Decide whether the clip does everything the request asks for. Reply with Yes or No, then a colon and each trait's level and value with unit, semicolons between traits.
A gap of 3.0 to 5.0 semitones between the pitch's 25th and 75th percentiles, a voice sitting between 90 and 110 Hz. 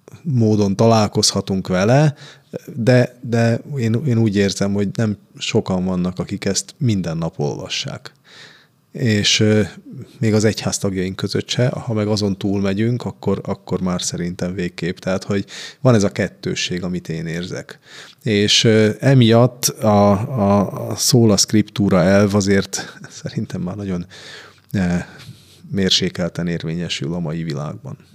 Yes: average, 3.7 semitones; low, 105 Hz